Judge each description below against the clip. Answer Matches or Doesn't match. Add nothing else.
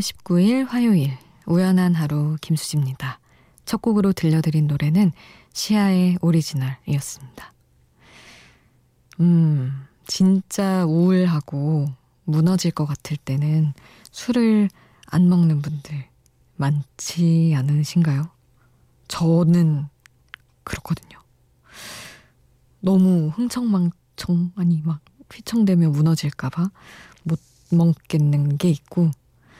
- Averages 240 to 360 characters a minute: Doesn't match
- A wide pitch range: Doesn't match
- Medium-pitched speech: Matches